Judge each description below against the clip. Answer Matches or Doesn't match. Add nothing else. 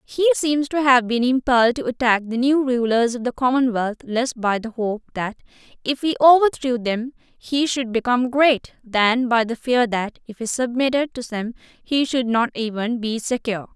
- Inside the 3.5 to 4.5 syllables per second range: Doesn't match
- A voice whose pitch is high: Matches